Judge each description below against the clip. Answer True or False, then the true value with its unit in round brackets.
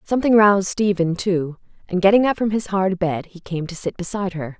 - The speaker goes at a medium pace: False (220 wpm)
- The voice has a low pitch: False (190 Hz)